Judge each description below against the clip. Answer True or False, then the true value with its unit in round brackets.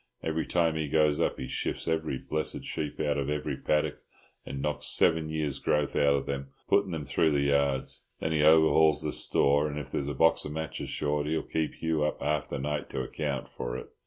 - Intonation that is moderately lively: False (1.7 semitones)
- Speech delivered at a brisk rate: True (220 wpm)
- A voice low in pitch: True (75 Hz)